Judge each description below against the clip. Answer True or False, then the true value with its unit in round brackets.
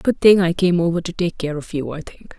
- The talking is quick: True (300 wpm)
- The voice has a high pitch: False (175 Hz)